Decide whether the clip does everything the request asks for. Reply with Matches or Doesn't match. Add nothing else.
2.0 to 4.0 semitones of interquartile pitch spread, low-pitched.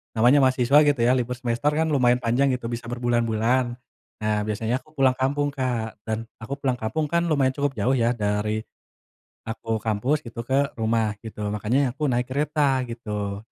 Matches